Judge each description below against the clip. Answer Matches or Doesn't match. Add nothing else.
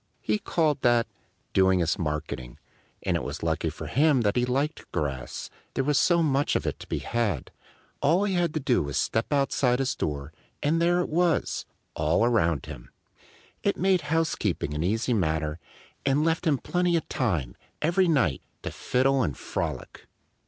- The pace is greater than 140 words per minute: Matches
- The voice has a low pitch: Matches